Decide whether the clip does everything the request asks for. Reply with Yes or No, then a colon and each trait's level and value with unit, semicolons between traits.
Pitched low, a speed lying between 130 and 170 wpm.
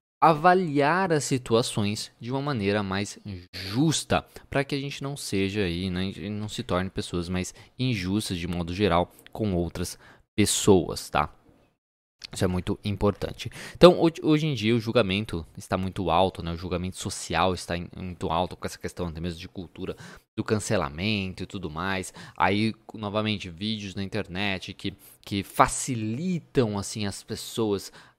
Yes: low, 100 Hz; average, 155 wpm